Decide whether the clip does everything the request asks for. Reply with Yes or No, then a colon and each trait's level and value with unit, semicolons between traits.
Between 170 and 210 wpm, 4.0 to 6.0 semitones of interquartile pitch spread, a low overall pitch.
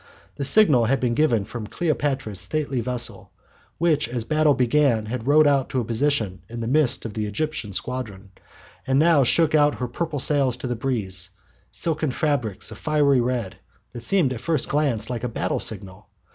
Yes: average, 185 wpm; average, 4.6 semitones; low, 130 Hz